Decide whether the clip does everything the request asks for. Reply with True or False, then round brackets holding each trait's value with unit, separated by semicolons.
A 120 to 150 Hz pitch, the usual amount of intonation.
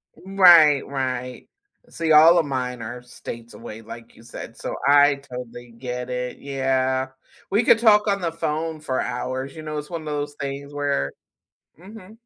True (140 Hz; 4.3 semitones)